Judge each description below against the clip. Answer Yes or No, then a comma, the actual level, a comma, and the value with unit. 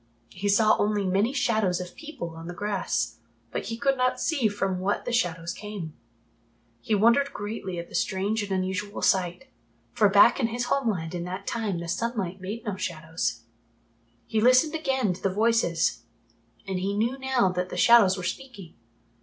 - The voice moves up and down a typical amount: Yes, average, 4.2 semitones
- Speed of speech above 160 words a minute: Yes, average, 180 wpm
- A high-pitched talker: Yes, high, 205 Hz